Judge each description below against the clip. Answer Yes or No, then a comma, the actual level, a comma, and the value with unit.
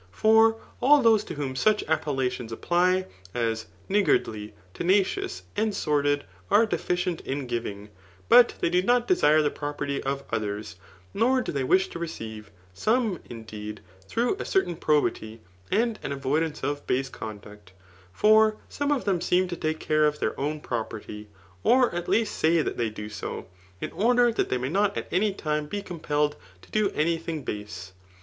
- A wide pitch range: Yes, wide, 9.0 semitones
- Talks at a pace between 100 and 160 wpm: No, average, 175 wpm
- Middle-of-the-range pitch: Yes, medium, 155 Hz